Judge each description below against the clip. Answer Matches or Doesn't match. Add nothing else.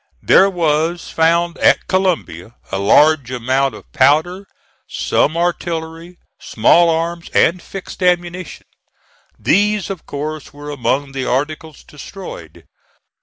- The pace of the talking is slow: Matches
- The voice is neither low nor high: Matches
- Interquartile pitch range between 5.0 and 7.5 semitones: Doesn't match